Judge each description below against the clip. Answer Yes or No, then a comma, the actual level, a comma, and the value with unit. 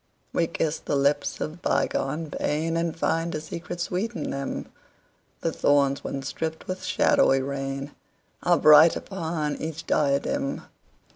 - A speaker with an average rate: No, slow, 125 wpm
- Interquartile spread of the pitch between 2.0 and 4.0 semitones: Yes, average, 3.0 semitones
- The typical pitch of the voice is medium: Yes, medium, 155 Hz